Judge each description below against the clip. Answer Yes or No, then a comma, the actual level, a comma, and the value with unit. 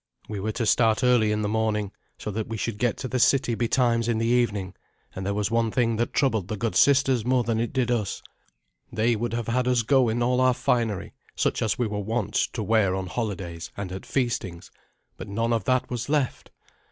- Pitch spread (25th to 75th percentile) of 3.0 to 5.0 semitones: No, narrow, 2.6 semitones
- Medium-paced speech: No, fast, 225 wpm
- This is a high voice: No, low, 115 Hz